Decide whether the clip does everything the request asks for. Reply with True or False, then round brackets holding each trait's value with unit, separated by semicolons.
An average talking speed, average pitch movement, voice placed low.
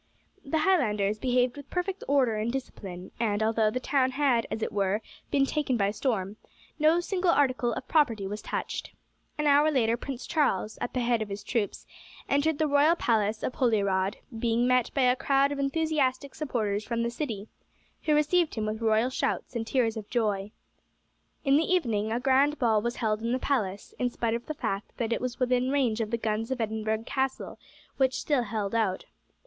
False (195 wpm; 4.3 semitones; 240 Hz)